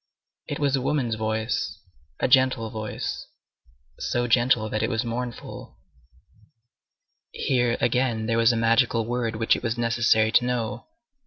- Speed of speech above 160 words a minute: No, average, 145 wpm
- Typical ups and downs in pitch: No, narrow, 1.8 semitones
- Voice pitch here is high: No, low, 115 Hz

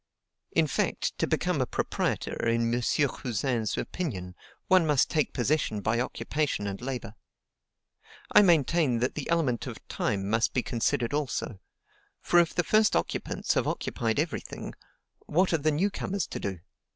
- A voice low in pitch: Yes, low, 130 Hz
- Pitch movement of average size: No, wide, 5.7 semitones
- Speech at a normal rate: Yes, average, 160 wpm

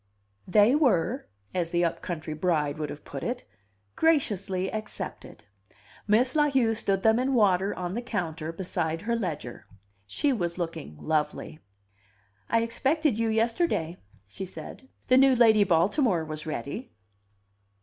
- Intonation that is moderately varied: No, wide, 6.4 semitones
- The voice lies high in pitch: Yes, high, 195 Hz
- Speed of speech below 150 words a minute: Yes, average, 140 wpm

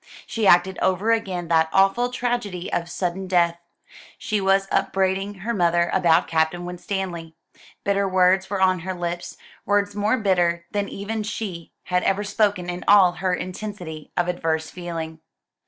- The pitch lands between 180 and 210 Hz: Yes, medium, 185 Hz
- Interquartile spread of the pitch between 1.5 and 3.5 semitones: Yes, narrow, 2.6 semitones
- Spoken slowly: No, average, 155 wpm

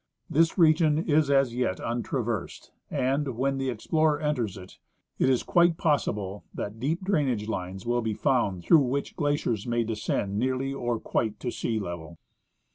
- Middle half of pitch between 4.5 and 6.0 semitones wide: Yes, average, 5.2 semitones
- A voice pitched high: No, low, 125 Hz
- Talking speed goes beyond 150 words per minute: Yes, average, 160 wpm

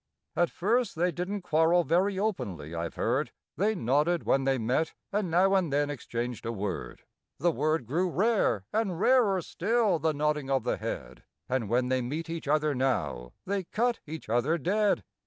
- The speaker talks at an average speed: Yes, average, 175 wpm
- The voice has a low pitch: No, medium, 160 Hz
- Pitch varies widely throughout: Yes, wide, 6.6 semitones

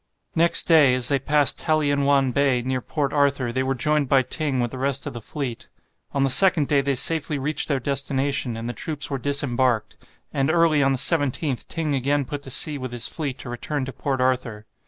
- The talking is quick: Yes, fast, 215 wpm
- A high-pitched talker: No, medium, 140 Hz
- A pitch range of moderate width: No, narrow, 2.2 semitones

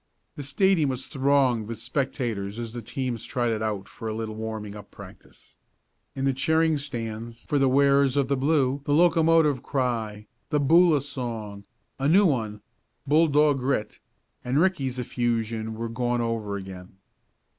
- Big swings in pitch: No, average, 4.2 semitones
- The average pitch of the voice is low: Yes, low, 125 Hz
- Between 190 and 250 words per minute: No, average, 155 wpm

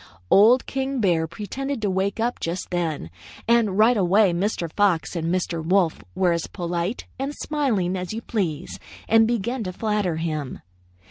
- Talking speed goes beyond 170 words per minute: No, average, 160 wpm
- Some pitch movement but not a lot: Yes, average, 4.7 semitones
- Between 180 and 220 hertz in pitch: Yes, high, 190 Hz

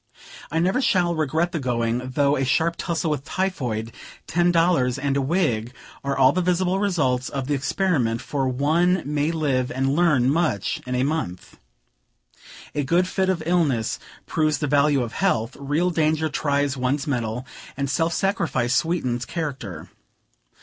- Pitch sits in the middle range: Yes, medium, 145 Hz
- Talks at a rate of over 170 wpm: No, average, 160 wpm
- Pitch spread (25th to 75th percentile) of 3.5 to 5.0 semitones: Yes, average, 4.7 semitones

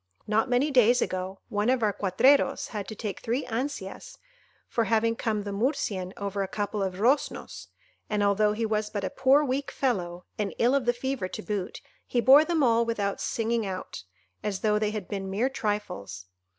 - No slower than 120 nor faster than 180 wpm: No, average, 190 wpm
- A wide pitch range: No, average, 3.6 semitones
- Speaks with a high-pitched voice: Yes, high, 215 Hz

